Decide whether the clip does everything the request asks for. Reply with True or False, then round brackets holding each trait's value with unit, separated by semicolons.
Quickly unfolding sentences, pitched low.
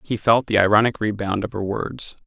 True (210 wpm; 105 Hz)